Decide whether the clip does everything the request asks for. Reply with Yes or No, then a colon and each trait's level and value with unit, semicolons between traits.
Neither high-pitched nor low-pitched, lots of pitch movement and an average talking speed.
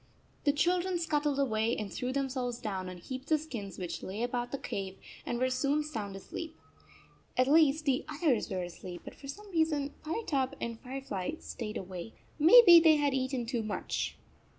No: very high, 260 Hz; wide, 5.7 semitones; average, 175 wpm